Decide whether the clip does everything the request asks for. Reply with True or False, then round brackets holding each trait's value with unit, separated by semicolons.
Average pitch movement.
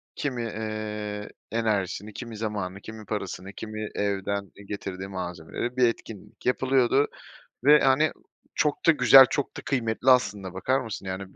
True (4.3 semitones)